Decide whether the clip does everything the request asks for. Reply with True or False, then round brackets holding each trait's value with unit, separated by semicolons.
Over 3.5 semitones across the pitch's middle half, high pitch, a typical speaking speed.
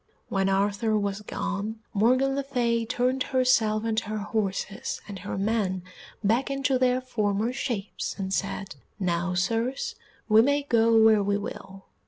True (4.0 semitones; 220 Hz; 150 wpm)